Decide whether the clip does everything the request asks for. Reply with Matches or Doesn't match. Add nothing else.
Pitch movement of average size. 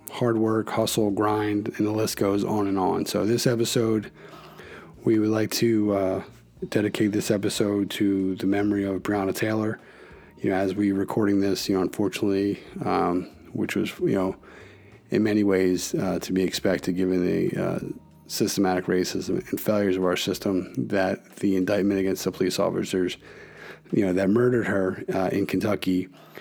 Doesn't match